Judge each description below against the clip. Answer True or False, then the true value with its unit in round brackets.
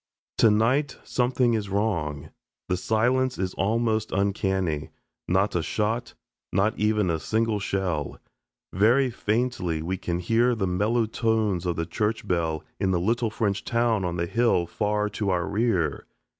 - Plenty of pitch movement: False (4.0 semitones)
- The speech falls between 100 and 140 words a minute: False (150 wpm)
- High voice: False (105 Hz)